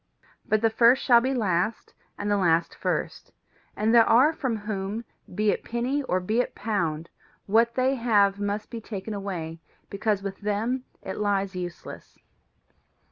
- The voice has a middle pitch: No, high, 210 Hz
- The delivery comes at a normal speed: Yes, average, 160 wpm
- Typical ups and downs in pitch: Yes, average, 3.2 semitones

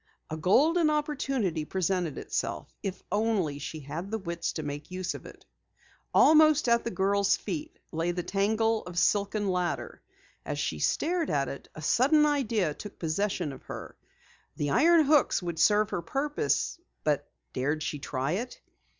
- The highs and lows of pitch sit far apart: Yes, wide, 7.9 semitones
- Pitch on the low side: No, high, 195 Hz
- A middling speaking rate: Yes, average, 160 wpm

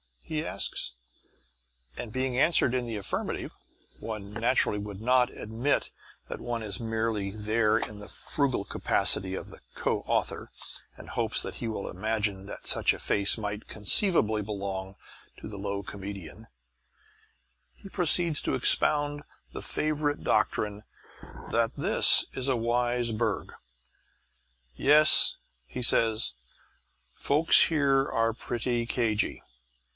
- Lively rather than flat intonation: No, average, 3.9 semitones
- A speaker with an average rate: No, slow, 125 wpm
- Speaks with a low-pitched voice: Yes, low, 115 Hz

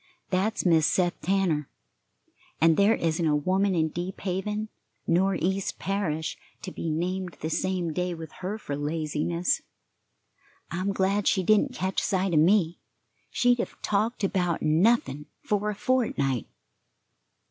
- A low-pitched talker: No, medium, 185 Hz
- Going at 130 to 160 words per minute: Yes, average, 140 wpm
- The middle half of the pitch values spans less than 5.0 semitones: Yes, average, 3.7 semitones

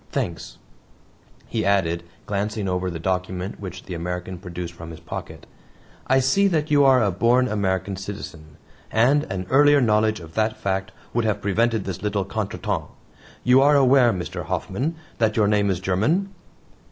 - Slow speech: No, average, 165 wpm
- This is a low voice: Yes, low, 100 Hz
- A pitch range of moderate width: Yes, average, 4.7 semitones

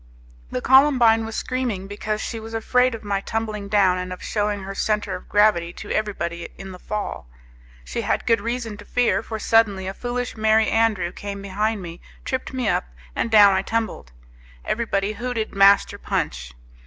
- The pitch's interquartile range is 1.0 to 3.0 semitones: Yes, narrow, 2.6 semitones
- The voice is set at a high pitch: Yes, high, 210 Hz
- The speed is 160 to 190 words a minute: Yes, average, 180 wpm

